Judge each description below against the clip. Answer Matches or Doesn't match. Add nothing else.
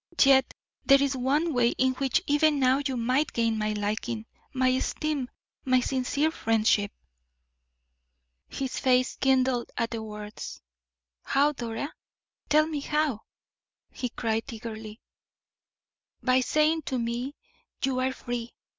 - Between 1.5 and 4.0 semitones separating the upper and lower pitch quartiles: Matches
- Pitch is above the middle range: Matches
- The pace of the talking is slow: Matches